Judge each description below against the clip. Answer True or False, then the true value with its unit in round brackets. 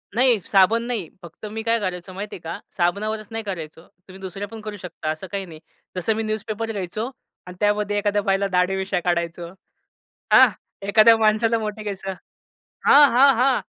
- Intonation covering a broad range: False (3.2 semitones)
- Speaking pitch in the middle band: False (205 Hz)